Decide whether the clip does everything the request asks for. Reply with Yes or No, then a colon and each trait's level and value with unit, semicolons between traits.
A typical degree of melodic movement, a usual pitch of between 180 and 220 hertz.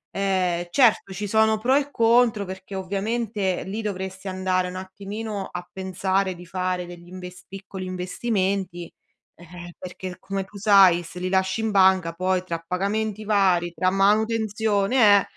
No: narrow, 2.3 semitones; high, 190 Hz